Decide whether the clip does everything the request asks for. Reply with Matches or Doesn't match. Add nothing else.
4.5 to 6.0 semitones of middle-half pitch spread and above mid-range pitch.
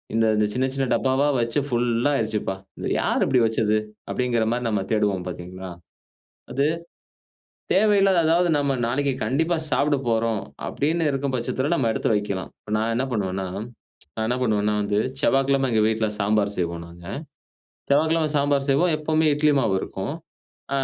Doesn't match